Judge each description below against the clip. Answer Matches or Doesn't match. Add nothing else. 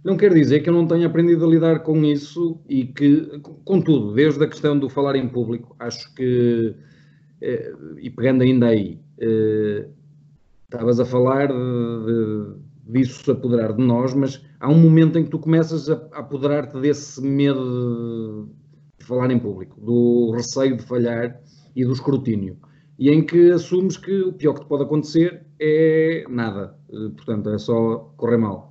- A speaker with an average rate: Matches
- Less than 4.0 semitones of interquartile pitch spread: Doesn't match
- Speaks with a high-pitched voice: Doesn't match